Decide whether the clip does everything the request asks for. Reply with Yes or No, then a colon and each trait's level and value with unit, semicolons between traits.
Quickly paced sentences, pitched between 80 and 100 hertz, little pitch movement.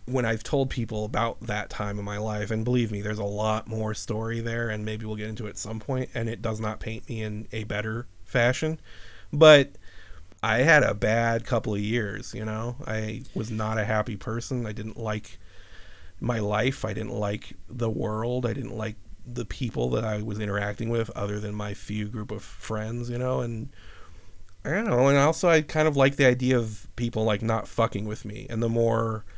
No: fast, 215 wpm; low, 110 Hz; narrow, 2.3 semitones